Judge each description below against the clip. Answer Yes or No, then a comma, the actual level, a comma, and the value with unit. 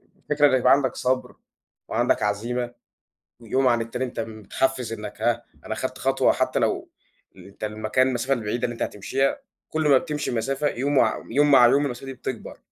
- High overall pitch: No, low, 125 Hz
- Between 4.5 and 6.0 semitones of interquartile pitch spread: No, average, 2.9 semitones